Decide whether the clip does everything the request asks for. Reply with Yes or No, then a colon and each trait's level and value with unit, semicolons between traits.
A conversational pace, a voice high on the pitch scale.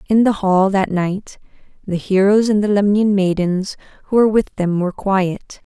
Yes: average, 180 wpm; high, 195 Hz